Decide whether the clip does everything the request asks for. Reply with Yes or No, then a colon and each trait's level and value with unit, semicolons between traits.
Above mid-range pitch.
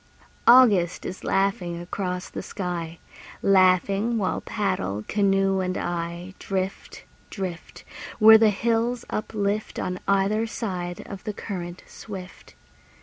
Yes: high, 195 Hz